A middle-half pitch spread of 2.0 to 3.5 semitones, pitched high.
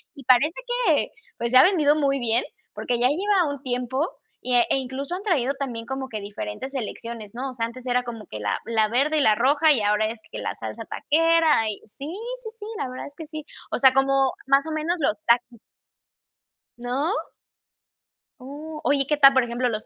No: average, 4.0 semitones; very high, 265 Hz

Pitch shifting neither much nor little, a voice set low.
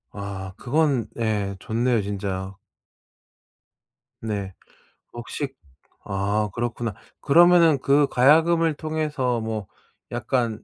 No: wide, 5.9 semitones; low, 120 Hz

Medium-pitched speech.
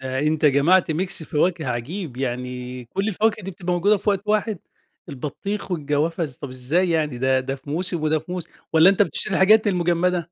Yes: medium, 165 Hz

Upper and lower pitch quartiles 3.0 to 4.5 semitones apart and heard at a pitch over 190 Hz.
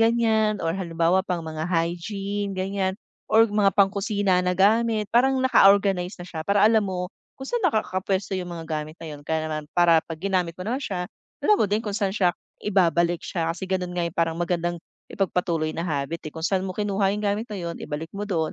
No: average, 3.3 semitones; medium, 185 Hz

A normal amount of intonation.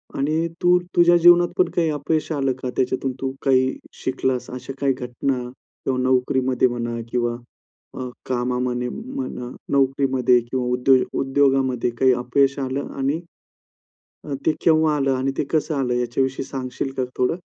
No: narrow, 2.0 semitones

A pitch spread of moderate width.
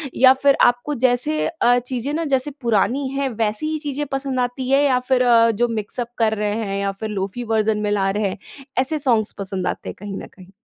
Yes: average, 4.1 semitones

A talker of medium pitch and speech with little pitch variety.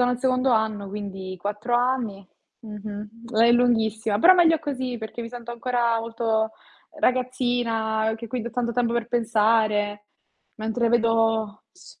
No: high, 230 Hz; narrow, 2.0 semitones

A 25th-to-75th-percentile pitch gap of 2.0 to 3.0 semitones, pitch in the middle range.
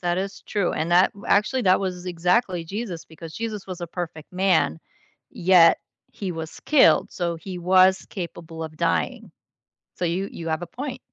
Yes: average, 2.7 semitones; medium, 180 Hz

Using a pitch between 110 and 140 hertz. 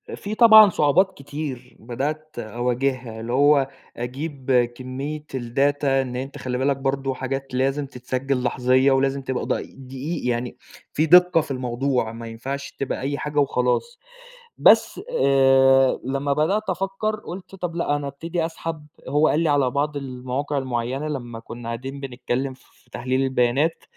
Yes: low, 135 Hz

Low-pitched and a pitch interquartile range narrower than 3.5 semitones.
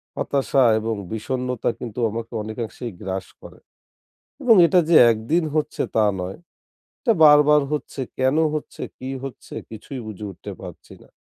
No: low, 125 Hz; average, 5.1 semitones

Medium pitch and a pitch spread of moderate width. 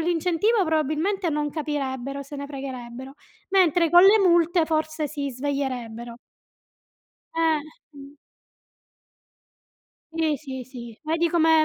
No: very high, 305 Hz; average, 3.4 semitones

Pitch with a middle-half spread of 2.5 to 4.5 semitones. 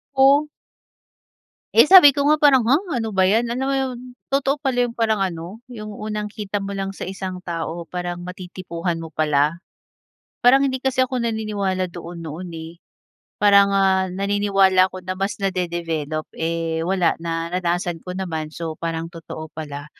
No: average, 4.9 semitones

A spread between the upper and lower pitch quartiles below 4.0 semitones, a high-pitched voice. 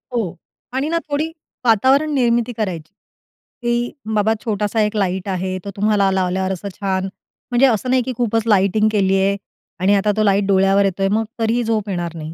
Yes: average, 3.4 semitones; high, 205 Hz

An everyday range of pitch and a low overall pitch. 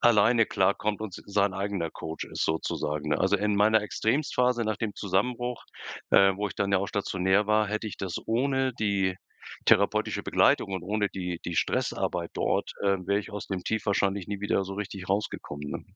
No: narrow, 2.1 semitones; low, 100 Hz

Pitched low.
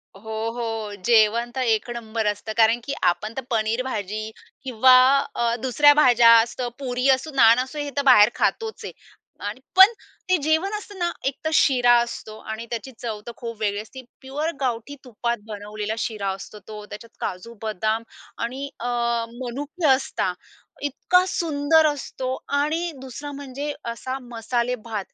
No: high, 240 Hz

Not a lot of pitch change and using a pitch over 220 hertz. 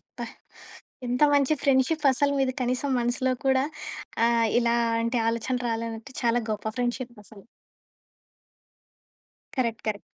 Yes: narrow, 2.2 semitones; high, 240 Hz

